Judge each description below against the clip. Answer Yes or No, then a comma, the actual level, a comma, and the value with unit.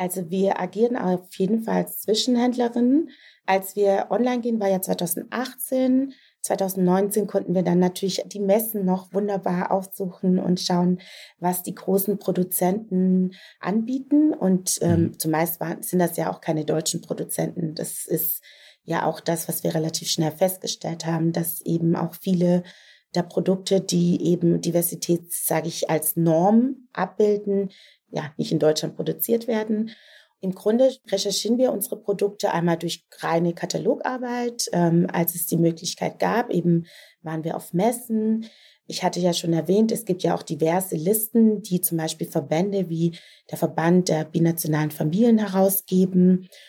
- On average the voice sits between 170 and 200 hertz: Yes, medium, 185 Hz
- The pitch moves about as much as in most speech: Yes, average, 3.5 semitones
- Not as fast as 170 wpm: Yes, average, 150 wpm